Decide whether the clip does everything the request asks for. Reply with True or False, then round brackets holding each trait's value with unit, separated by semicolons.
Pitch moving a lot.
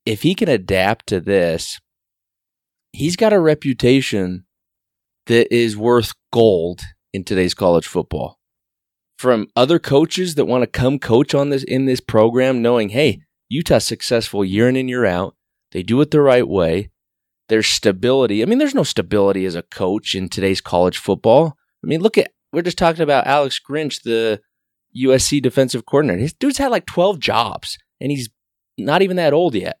True (5.7 semitones)